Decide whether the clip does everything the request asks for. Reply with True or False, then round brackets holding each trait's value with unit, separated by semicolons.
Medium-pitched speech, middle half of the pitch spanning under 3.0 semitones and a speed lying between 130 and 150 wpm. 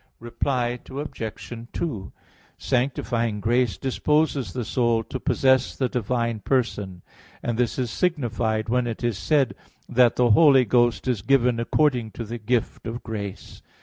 False (120 Hz; 2.5 semitones; 145 wpm)